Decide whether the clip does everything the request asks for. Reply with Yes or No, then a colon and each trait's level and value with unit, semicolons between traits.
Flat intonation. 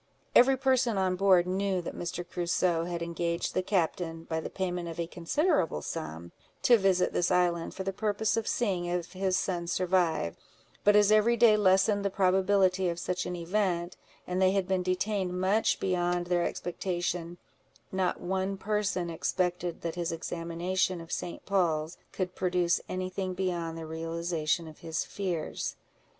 Yes: narrow, 2.0 semitones